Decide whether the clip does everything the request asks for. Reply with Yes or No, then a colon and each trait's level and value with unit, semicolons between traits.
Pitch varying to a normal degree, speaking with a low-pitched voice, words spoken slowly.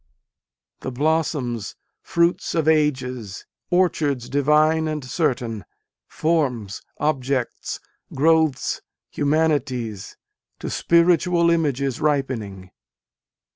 No: average, 4.2 semitones; medium, 145 Hz; slow, 75 wpm